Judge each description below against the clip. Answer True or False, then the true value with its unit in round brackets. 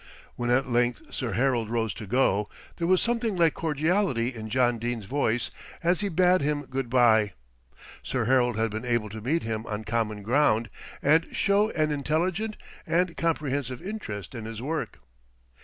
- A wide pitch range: True (6.3 semitones)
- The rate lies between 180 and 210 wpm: False (170 wpm)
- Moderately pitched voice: False (125 Hz)